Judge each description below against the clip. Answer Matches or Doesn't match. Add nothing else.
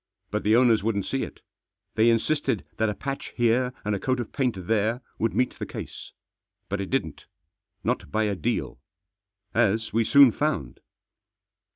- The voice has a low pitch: Matches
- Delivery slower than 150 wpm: Doesn't match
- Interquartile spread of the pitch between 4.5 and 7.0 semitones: Doesn't match